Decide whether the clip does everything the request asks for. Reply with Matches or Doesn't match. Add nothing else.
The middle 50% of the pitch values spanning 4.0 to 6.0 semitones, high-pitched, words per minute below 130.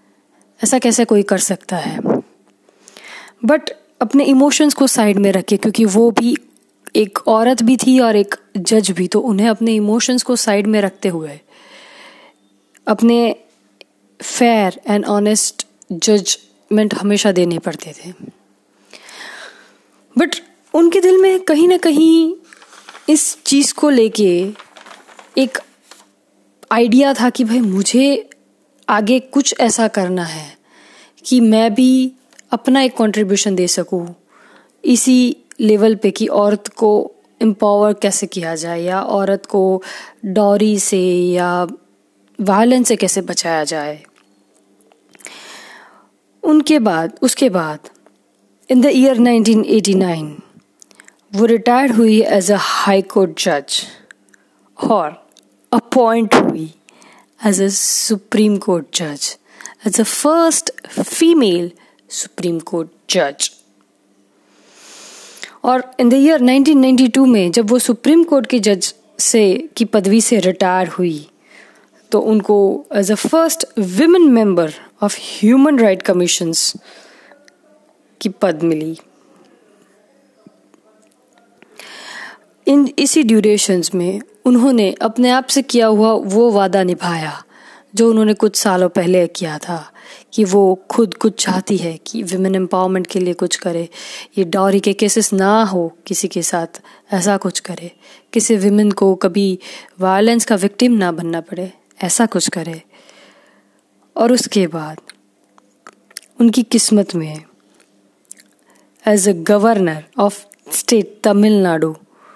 Matches